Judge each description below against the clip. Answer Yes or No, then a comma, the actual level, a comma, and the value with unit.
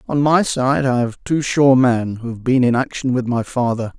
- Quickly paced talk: Yes, fast, 240 wpm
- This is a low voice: Yes, low, 125 Hz